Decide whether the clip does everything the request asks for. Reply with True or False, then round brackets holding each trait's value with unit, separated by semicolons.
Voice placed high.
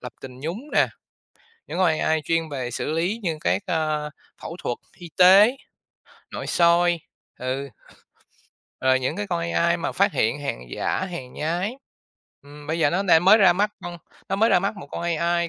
False (165 Hz)